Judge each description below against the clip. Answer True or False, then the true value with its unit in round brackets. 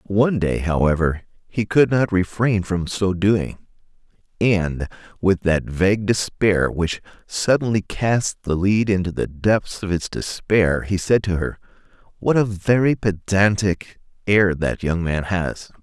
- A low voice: True (95 Hz)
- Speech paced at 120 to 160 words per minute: True (150 wpm)